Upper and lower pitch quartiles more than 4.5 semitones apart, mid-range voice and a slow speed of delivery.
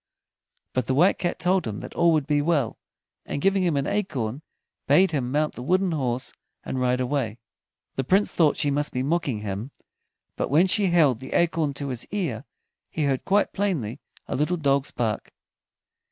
No: average, 5.2 semitones; medium, 145 Hz; average, 185 wpm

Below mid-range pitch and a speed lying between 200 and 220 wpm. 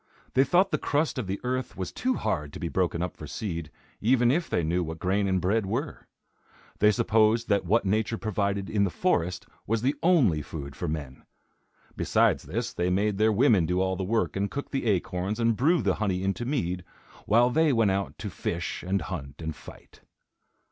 Yes: low, 100 Hz; fast, 205 wpm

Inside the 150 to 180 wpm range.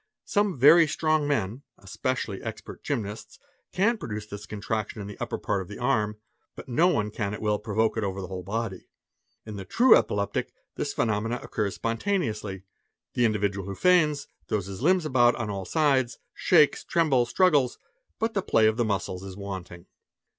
Yes: average, 175 wpm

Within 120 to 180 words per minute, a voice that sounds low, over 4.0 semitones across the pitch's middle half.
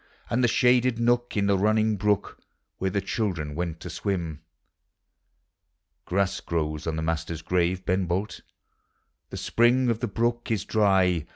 Yes: average, 155 wpm; low, 100 Hz; average, 4.9 semitones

